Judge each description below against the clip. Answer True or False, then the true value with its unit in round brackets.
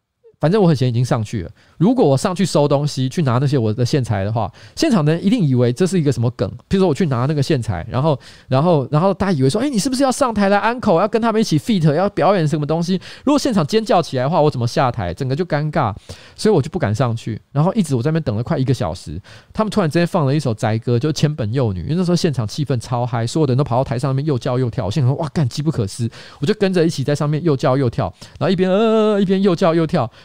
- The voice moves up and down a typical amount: False (6.7 semitones)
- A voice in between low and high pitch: True (150 Hz)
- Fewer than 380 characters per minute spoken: False (430 characters per minute)